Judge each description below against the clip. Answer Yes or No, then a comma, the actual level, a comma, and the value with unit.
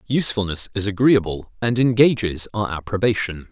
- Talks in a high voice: No, low, 105 Hz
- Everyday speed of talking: No, slow, 120 wpm